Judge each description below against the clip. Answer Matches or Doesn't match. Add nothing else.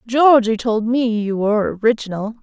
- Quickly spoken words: Doesn't match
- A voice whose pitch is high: Matches